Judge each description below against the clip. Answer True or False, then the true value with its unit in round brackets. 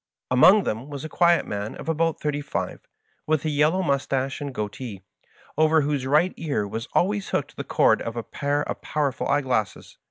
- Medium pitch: True (145 Hz)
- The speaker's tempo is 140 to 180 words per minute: False (190 wpm)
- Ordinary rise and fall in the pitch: True (3.6 semitones)